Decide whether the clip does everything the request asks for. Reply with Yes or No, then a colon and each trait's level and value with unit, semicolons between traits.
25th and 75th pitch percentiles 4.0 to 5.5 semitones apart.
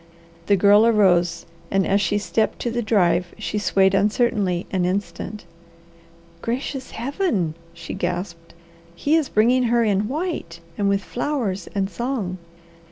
Yes: average, 4.5 semitones